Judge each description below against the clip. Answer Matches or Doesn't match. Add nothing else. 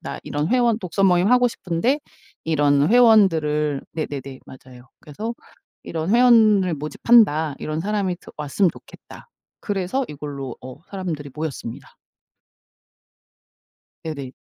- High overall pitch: Doesn't match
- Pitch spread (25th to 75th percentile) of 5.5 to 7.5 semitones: Matches